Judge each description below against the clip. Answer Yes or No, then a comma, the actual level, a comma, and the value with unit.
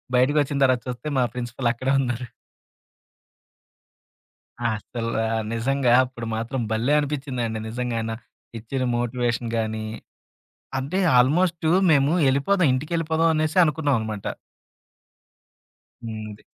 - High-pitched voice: No, low, 125 Hz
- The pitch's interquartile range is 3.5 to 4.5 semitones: Yes, average, 3.9 semitones